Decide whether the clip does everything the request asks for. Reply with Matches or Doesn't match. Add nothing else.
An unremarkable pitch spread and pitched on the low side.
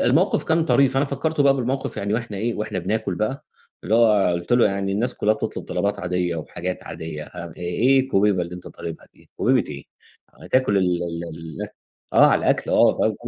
Doesn't match